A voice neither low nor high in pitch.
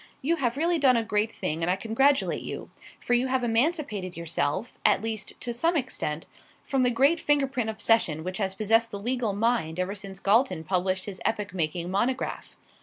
No: high, 225 Hz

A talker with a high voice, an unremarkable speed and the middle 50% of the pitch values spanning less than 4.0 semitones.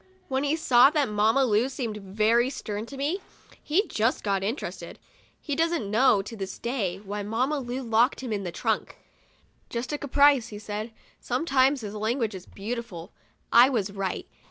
No: high, 235 Hz; average, 175 wpm; average, 4.5 semitones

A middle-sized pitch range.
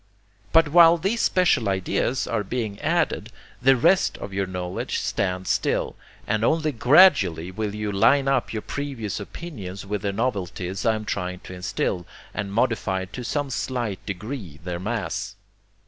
No: wide, 5.8 semitones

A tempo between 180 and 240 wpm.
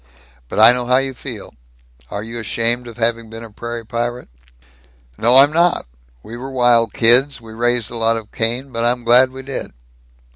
Yes: average, 190 wpm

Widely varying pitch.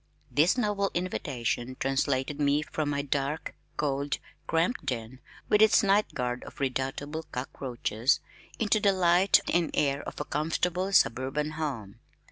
No: average, 4.9 semitones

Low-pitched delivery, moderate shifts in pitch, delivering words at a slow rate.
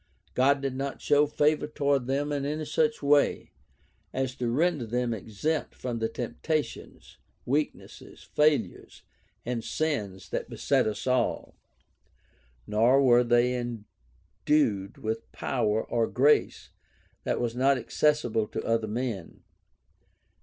Yes: low, 125 Hz; average, 4.2 semitones; slow, 125 wpm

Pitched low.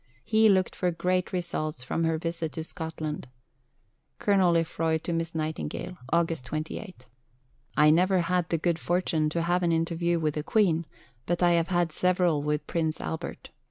No: medium, 165 Hz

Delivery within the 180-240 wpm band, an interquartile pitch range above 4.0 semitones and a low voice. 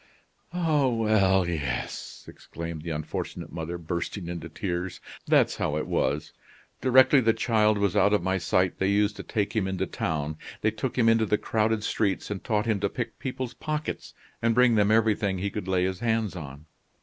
Yes: average, 185 wpm; average, 4.4 semitones; low, 100 Hz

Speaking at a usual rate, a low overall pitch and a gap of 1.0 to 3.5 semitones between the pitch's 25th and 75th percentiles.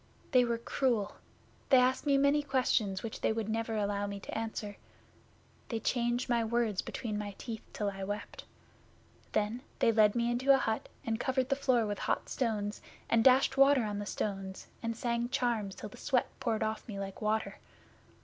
No: average, 190 wpm; high, 225 Hz; average, 3.2 semitones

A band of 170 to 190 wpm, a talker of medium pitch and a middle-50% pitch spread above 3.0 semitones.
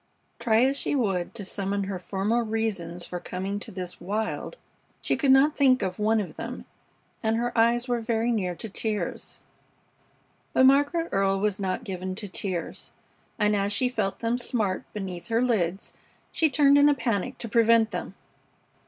No: average, 175 wpm; high, 220 Hz; average, 3.8 semitones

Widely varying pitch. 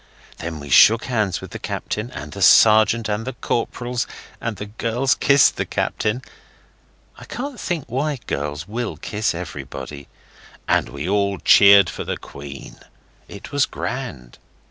Yes: wide, 6.5 semitones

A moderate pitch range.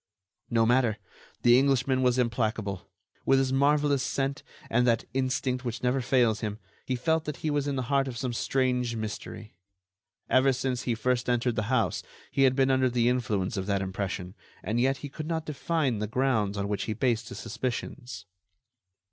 Yes: average, 3.1 semitones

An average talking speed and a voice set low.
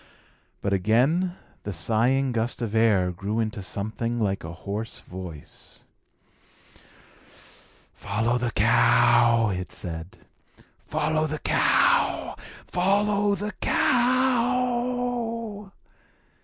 No: slow, 90 wpm; low, 120 Hz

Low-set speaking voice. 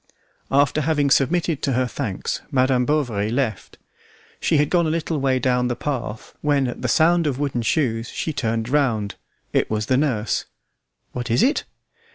Yes: low, 130 Hz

